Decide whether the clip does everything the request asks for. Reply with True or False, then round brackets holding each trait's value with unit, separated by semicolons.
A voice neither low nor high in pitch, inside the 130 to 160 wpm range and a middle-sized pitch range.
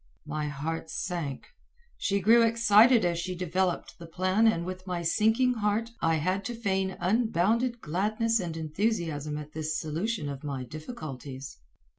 False (180 Hz; 150 wpm; 5.9 semitones)